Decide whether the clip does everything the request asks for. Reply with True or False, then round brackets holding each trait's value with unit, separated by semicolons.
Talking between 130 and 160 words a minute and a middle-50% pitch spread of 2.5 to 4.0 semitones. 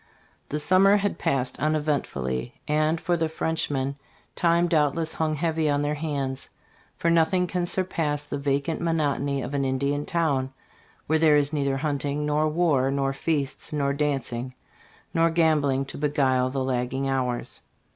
True (155 wpm; 2.9 semitones)